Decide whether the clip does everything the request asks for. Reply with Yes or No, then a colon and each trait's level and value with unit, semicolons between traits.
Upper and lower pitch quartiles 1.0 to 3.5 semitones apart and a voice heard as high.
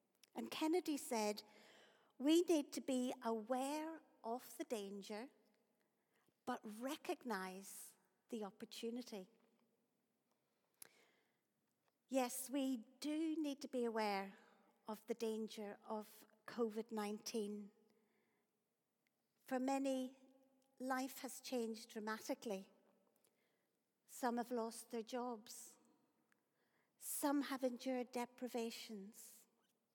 Yes: average, 3.2 semitones; high, 230 Hz